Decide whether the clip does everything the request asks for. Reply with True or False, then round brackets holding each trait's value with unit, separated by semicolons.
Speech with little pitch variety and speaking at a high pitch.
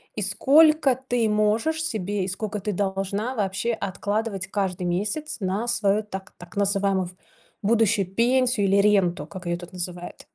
False (3.1 semitones; 205 Hz)